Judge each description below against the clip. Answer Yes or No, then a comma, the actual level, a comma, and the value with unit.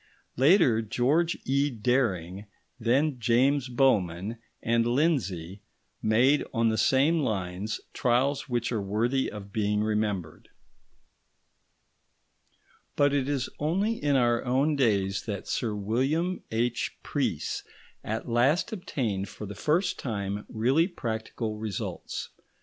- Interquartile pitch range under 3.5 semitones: No, average, 4.7 semitones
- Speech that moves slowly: Yes, slow, 115 wpm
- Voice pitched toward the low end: Yes, low, 120 Hz